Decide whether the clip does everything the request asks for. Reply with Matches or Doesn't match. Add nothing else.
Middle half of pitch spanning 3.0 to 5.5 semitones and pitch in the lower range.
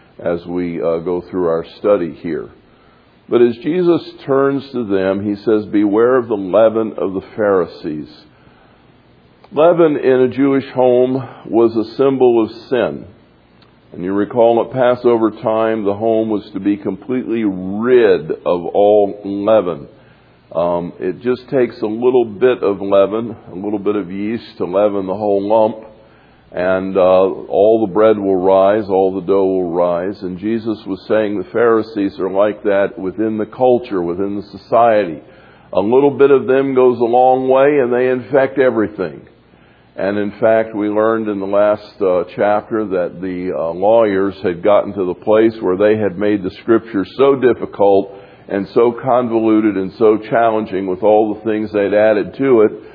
Matches